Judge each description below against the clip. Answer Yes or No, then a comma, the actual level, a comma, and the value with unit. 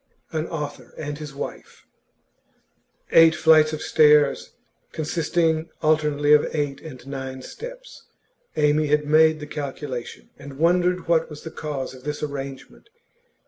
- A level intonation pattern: Yes, narrow, 1.8 semitones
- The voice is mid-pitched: Yes, medium, 150 Hz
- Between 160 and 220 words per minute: No, slow, 135 wpm